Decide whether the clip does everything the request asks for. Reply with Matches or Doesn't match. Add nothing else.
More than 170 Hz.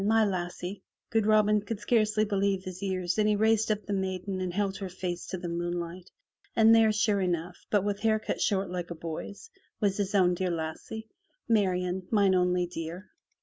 Matches